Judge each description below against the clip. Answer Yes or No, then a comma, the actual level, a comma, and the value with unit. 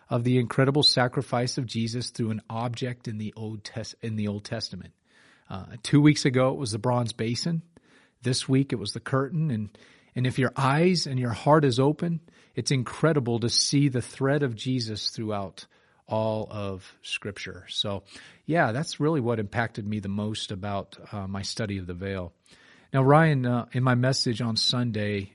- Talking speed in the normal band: Yes, average, 185 wpm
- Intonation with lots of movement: No, average, 3.8 semitones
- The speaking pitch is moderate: No, low, 120 Hz